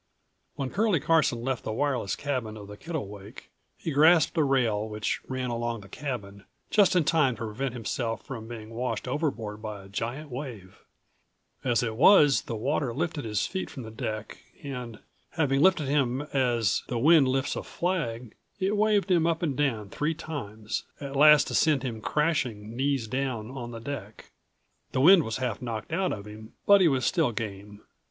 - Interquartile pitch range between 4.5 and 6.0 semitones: Yes, average, 5.2 semitones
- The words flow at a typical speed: Yes, average, 185 wpm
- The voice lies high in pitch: No, low, 130 Hz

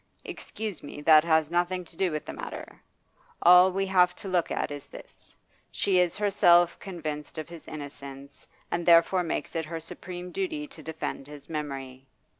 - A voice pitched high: No, medium, 170 Hz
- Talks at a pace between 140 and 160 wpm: No, average, 175 wpm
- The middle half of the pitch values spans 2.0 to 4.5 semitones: Yes, average, 3.2 semitones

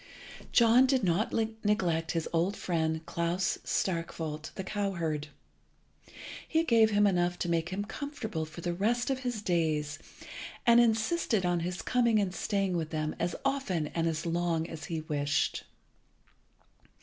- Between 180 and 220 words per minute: No, average, 150 wpm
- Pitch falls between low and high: Yes, medium, 180 Hz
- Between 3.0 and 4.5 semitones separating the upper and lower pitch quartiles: No, average, 5.1 semitones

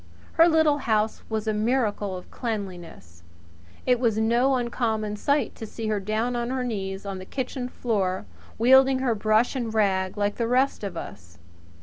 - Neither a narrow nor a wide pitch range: Yes, average, 3.5 semitones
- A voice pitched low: No, high, 220 Hz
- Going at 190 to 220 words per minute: No, average, 175 wpm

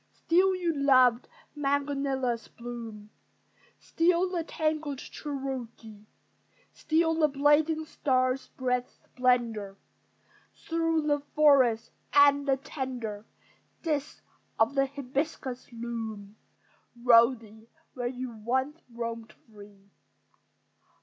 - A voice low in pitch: No, very high, 260 Hz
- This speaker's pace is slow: Yes, slow, 90 wpm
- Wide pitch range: No, average, 4.1 semitones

